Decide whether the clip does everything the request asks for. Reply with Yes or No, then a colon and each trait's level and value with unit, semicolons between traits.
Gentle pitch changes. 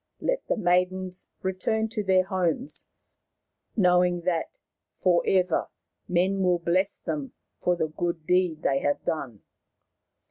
Yes: narrow, 1.7 semitones